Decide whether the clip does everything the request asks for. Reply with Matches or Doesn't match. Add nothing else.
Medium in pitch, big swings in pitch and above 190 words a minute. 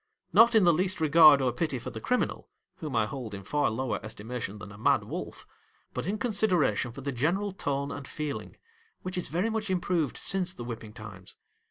Matches